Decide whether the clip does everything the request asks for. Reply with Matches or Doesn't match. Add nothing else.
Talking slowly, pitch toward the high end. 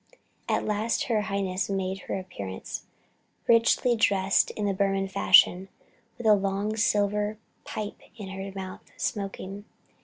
Matches